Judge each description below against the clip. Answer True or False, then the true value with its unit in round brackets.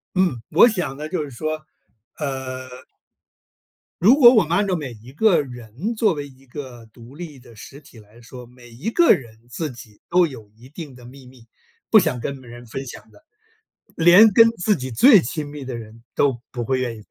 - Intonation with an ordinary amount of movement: False (6.1 semitones)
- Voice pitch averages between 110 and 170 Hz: True (135 Hz)